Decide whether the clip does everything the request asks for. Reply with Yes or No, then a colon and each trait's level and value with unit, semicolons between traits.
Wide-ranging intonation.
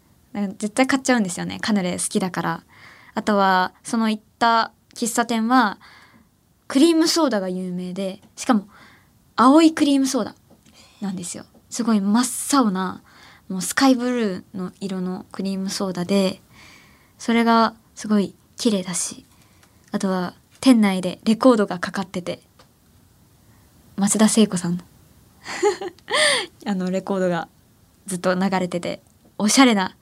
No: average, 4.4 semitones